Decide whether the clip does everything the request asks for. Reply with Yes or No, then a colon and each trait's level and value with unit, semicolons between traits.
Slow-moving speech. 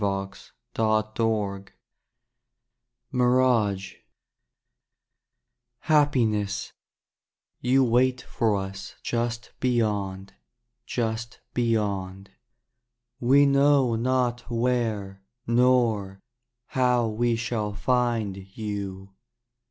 Yes: slow, 70 wpm